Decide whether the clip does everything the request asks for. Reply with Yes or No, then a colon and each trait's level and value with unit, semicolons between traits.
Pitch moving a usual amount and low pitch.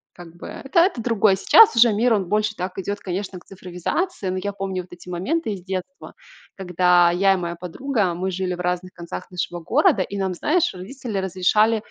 No: average, 3.2 semitones; high, 190 Hz